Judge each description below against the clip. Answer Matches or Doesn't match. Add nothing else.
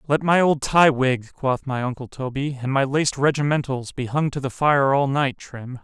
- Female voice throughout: Doesn't match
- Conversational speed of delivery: Doesn't match